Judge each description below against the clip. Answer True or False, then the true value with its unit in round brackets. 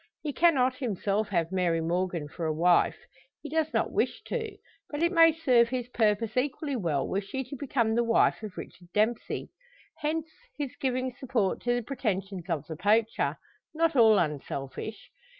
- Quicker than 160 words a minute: True (170 wpm)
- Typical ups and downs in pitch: False (6.6 semitones)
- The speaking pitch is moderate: False (230 Hz)